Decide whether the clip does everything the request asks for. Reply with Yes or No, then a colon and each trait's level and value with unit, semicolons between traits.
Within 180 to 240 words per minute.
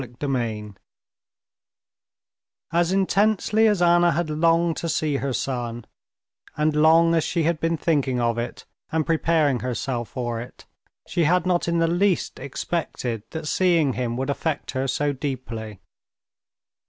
No: average, 145 wpm